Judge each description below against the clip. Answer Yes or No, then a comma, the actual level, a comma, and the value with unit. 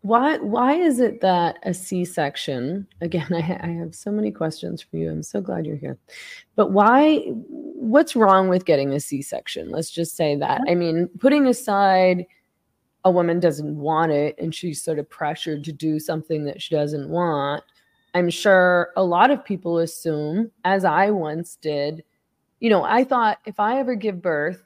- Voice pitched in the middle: Yes, medium, 175 Hz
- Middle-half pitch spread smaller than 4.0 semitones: No, average, 4.9 semitones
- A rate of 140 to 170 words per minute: No, average, 185 wpm